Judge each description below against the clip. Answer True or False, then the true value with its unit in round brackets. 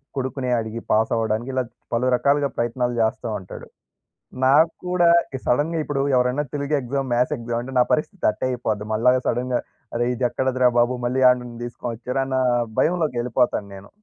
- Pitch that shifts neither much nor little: False (2.2 semitones)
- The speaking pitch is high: False (125 Hz)